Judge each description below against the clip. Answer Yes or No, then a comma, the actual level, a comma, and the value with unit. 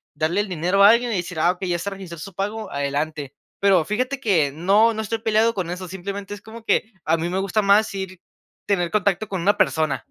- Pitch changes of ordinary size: Yes, average, 3.6 semitones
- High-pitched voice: Yes, high, 195 Hz